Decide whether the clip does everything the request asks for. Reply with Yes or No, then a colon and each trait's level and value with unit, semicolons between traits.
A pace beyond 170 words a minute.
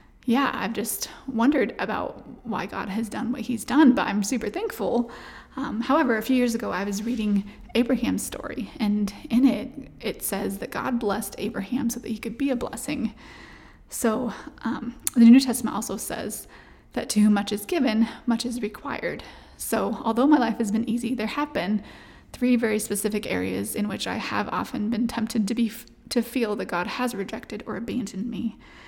Yes: average, 190 wpm